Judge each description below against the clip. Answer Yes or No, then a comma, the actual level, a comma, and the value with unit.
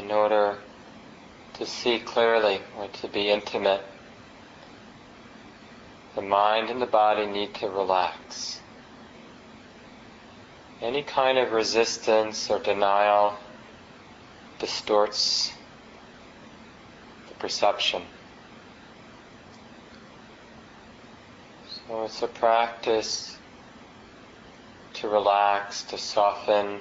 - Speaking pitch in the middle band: No, low, 105 Hz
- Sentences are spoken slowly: Yes, slow, 75 wpm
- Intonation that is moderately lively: No, narrow, 2.1 semitones